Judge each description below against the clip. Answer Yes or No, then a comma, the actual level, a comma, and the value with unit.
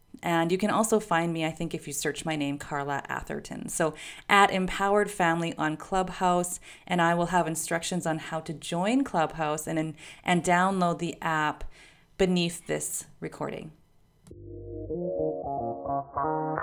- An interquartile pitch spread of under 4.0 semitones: Yes, average, 2.8 semitones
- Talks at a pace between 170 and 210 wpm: No, average, 140 wpm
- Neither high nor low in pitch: Yes, medium, 165 Hz